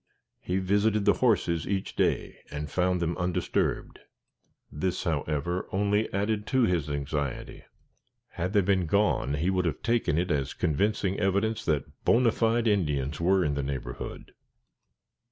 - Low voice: Yes, very low, 90 Hz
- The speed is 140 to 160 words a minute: Yes, average, 145 wpm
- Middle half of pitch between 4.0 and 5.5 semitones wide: Yes, average, 5.2 semitones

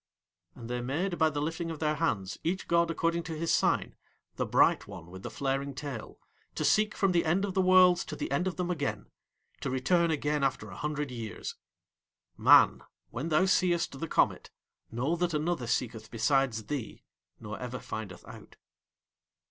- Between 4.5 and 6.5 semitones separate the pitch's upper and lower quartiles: Yes, wide, 5.5 semitones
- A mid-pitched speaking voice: Yes, medium, 150 Hz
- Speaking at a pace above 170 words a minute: Yes, average, 180 wpm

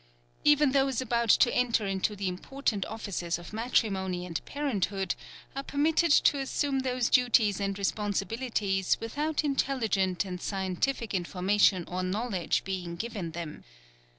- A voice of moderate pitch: No, high, 210 Hz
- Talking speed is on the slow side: Yes, slow, 130 wpm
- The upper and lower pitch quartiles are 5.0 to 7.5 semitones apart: Yes, wide, 5.5 semitones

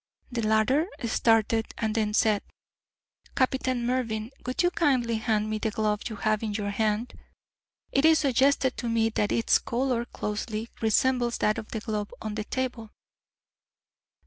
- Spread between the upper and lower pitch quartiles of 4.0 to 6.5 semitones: No, average, 2.8 semitones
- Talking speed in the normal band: Yes, average, 155 wpm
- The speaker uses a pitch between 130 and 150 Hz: No, high, 225 Hz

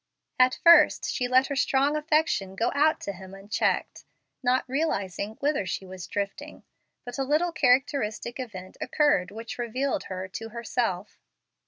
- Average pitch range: No, wide, 6.0 semitones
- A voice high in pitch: Yes, high, 245 Hz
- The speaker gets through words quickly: No, average, 150 wpm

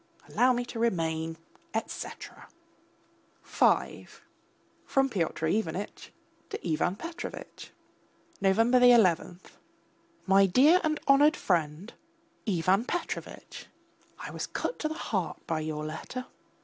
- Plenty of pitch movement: Yes, wide, 7.4 semitones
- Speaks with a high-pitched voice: Yes, high, 200 Hz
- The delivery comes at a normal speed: No, slow, 110 wpm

